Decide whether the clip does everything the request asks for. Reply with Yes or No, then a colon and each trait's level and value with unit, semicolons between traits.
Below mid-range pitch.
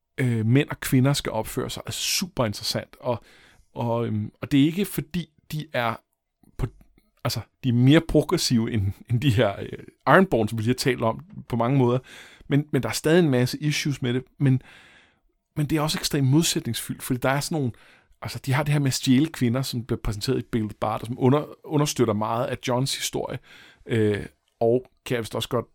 Yes: low, 130 Hz